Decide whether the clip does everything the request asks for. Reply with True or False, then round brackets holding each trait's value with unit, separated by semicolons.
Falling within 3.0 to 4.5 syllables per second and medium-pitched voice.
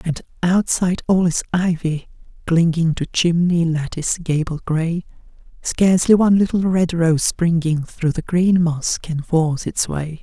True (4.4 syllables/s; 170 Hz)